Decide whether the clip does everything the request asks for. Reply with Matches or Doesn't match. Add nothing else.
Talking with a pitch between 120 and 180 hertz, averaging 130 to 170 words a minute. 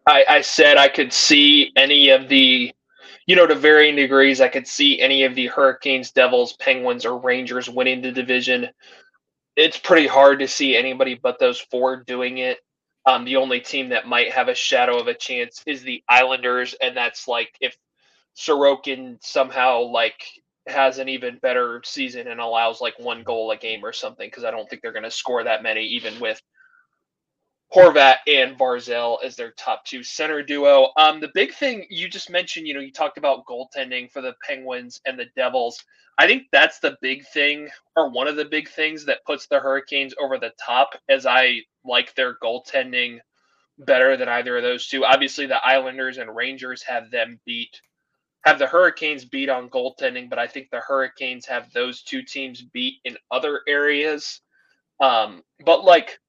Doesn't match